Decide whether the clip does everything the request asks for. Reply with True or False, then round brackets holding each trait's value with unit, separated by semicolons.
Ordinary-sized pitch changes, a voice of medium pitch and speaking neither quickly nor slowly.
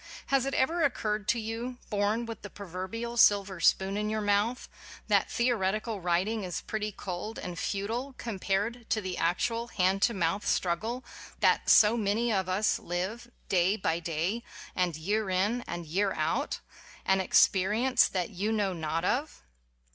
False (3.6 semitones; 205 Hz; 170 wpm)